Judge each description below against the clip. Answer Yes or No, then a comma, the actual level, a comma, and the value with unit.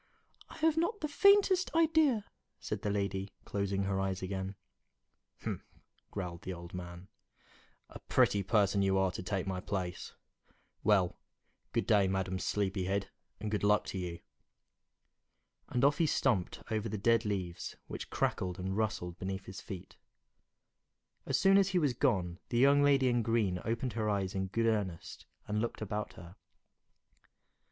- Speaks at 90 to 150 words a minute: No, average, 160 wpm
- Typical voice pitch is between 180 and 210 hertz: No, low, 100 Hz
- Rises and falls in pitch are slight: No, average, 3.9 semitones